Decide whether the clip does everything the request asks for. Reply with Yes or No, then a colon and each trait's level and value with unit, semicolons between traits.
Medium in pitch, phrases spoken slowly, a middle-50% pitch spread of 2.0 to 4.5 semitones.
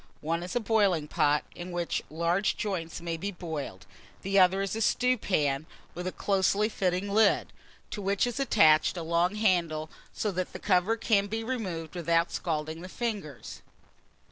No: medium, 180 Hz; average, 170 wpm; average, 3.7 semitones